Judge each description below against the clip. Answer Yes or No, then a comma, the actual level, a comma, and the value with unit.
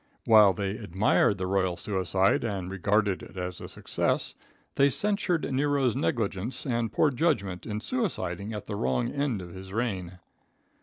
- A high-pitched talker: No, low, 105 Hz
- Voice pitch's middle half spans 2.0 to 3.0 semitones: No, wide, 5.4 semitones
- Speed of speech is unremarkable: Yes, average, 155 wpm